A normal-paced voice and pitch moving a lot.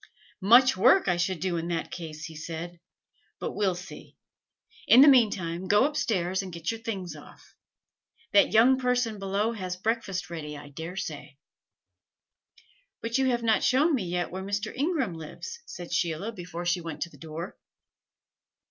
No: average, 175 wpm; average, 5.0 semitones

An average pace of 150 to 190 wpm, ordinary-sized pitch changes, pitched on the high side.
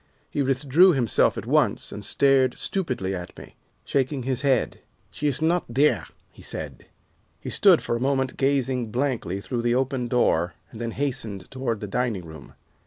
No: average, 175 wpm; average, 3.3 semitones; low, 125 Hz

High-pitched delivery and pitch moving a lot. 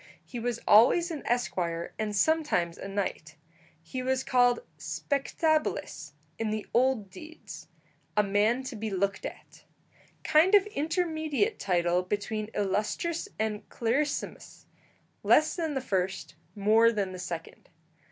Yes: high, 225 Hz; wide, 7.0 semitones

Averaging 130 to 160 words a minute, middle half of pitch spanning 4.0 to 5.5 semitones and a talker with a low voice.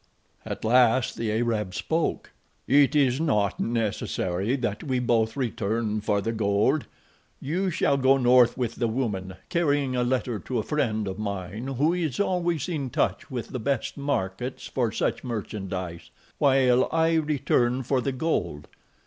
Yes: average, 155 wpm; average, 4.4 semitones; low, 125 Hz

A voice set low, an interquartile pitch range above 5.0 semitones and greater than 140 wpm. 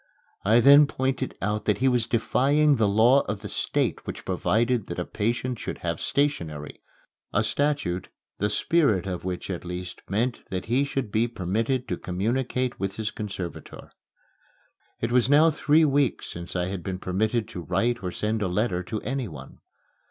Yes: low, 110 Hz; wide, 5.6 semitones; average, 175 wpm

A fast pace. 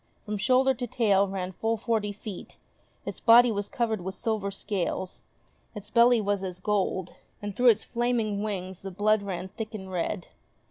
No: average, 175 wpm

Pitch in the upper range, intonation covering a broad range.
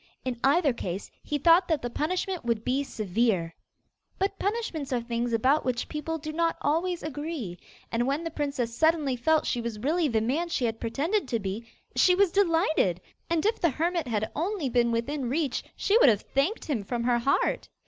Yes: very high, 280 Hz; wide, 5.9 semitones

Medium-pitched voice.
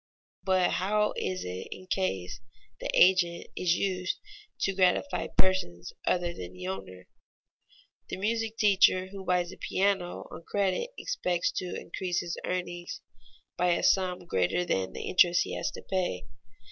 Yes: medium, 180 Hz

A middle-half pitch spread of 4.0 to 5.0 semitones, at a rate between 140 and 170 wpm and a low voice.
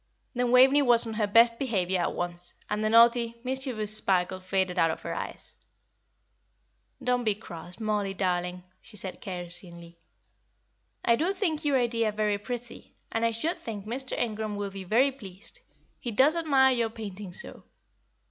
No: average, 4.5 semitones; average, 165 wpm; high, 215 Hz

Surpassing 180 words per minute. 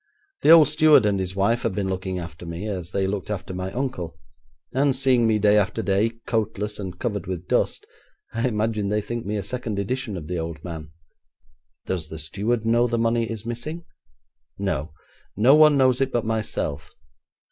Yes: average, 190 wpm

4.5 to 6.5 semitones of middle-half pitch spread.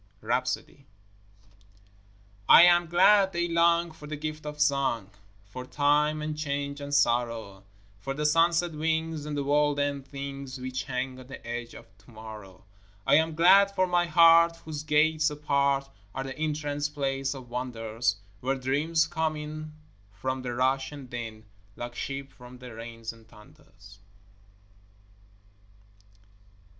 No: average, 3.6 semitones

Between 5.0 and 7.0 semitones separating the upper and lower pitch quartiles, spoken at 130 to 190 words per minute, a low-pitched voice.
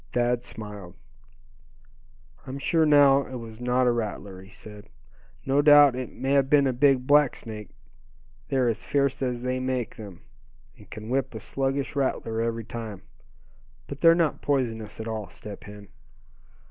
No: average, 3.7 semitones; average, 160 wpm; low, 125 Hz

